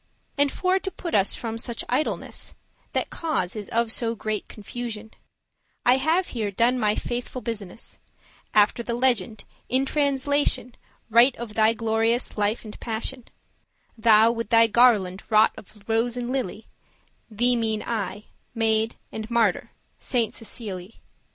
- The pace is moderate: Yes, average, 150 wpm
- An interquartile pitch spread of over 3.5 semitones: No, narrow, 2.4 semitones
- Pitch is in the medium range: No, high, 230 Hz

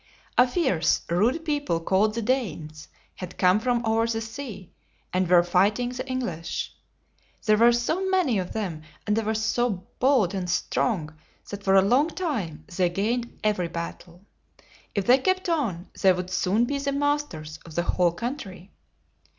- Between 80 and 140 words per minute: No, average, 170 wpm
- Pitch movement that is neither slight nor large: No, wide, 5.7 semitones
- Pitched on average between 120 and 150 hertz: No, high, 215 Hz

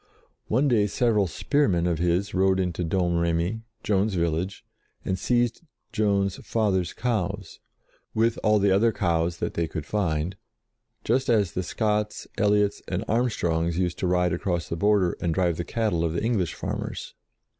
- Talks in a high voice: No, very low, 95 Hz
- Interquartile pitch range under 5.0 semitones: Yes, average, 3.8 semitones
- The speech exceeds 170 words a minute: No, average, 155 wpm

